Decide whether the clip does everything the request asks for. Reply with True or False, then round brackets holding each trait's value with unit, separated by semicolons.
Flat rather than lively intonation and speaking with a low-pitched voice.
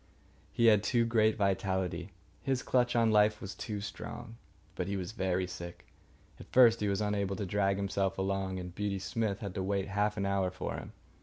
True (2.1 semitones; 100 Hz)